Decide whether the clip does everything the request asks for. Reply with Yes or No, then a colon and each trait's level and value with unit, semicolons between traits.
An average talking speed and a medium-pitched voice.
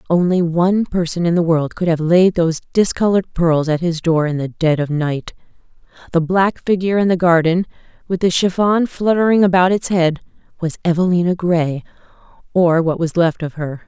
Yes: average, 175 wpm; medium, 175 Hz